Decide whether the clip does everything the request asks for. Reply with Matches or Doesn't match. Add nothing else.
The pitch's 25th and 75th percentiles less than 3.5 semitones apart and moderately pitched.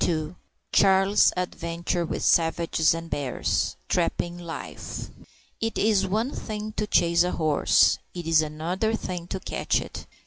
Matches